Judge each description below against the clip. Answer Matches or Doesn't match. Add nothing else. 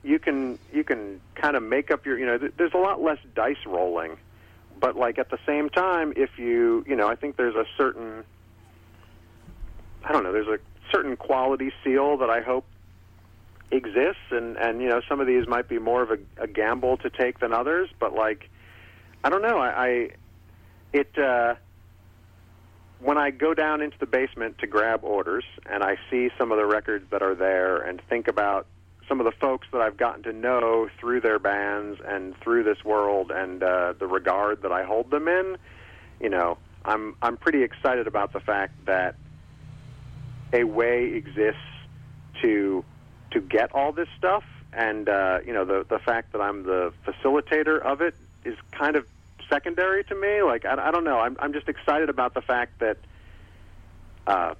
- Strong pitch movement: Matches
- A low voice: Matches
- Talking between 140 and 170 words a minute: Doesn't match